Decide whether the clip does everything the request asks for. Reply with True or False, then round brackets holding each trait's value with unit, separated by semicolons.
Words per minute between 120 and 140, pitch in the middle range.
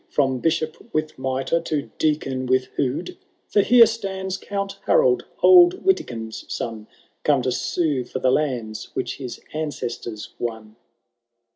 True (135 wpm; 145 Hz)